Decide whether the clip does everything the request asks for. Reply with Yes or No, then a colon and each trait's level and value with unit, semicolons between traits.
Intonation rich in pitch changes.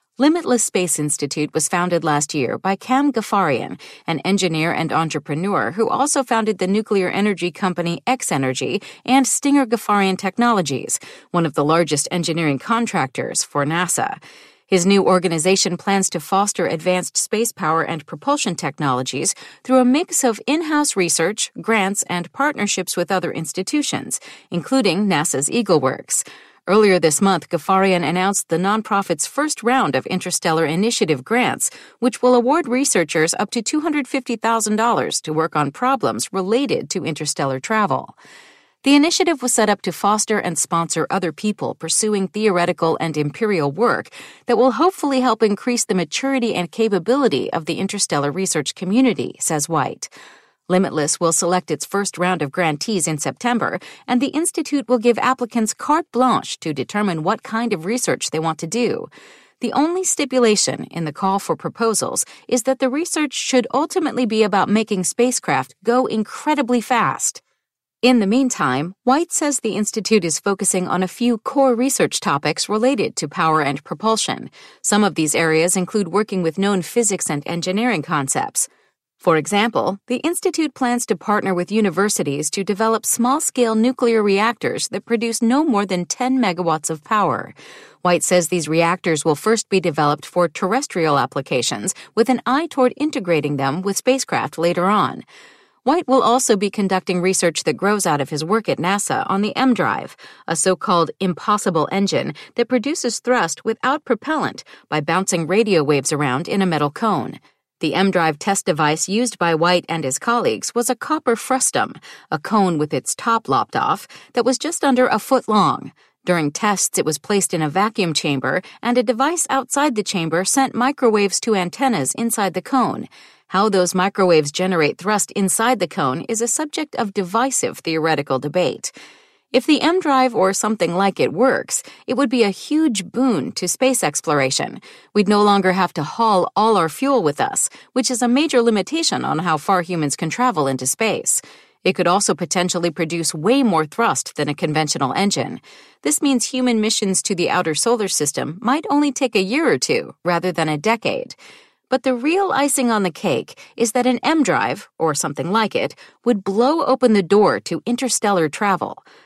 Yes: wide, 6.5 semitones